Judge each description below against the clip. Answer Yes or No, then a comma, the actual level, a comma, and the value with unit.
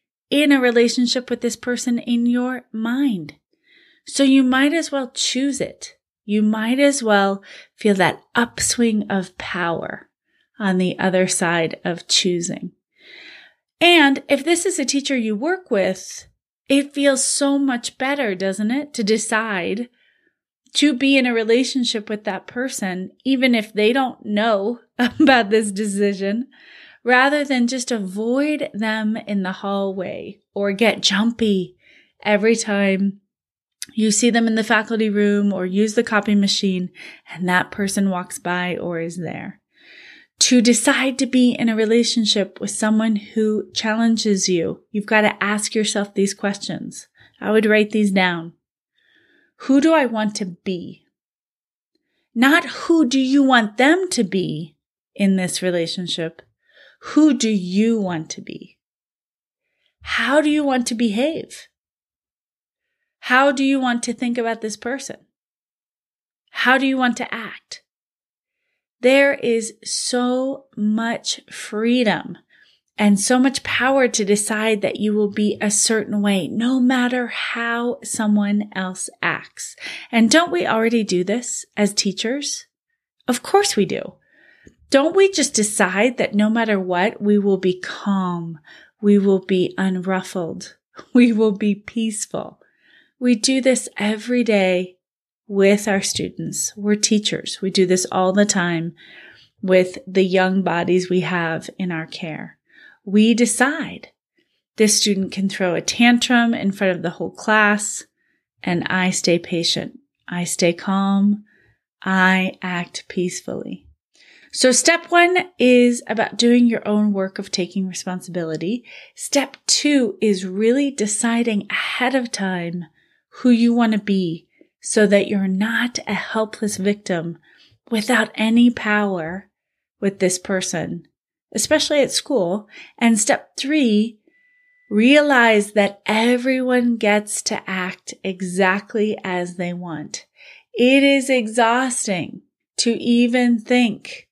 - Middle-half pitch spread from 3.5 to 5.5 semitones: Yes, average, 4.4 semitones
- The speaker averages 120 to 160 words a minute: Yes, average, 140 wpm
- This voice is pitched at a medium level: No, high, 220 Hz